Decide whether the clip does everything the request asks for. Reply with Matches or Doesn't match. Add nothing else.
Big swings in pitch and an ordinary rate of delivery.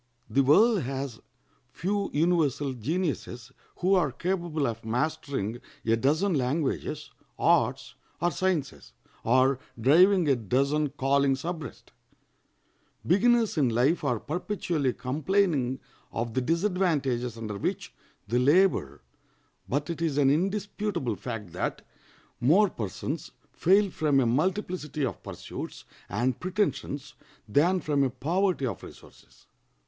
Doesn't match